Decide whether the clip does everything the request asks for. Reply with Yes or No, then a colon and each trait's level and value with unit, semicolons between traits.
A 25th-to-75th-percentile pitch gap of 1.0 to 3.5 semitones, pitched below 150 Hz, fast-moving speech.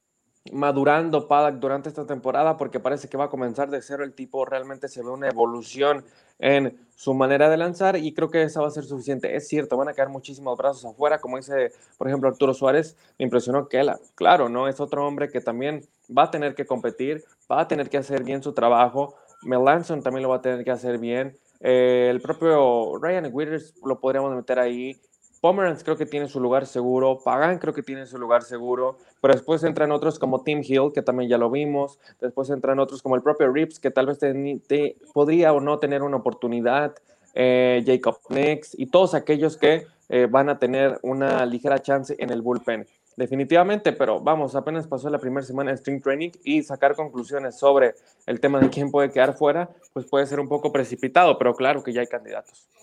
Yes: narrow, 2.4 semitones; medium, 140 Hz; fast, 210 wpm